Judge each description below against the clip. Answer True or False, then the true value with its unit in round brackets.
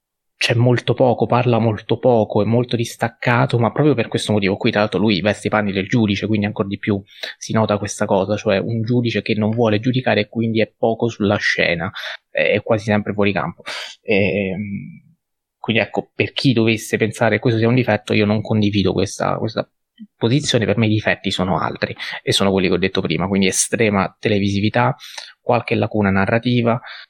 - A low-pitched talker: True (110 Hz)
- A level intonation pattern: True (2.3 semitones)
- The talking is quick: True (190 wpm)